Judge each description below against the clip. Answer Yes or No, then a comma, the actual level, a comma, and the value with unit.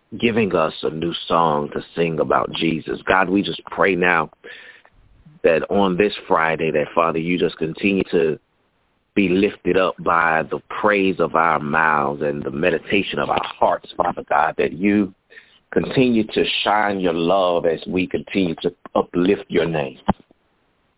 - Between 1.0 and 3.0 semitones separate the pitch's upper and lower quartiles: No, average, 3.8 semitones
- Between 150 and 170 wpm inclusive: Yes, average, 155 wpm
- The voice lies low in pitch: Yes, very low, 85 Hz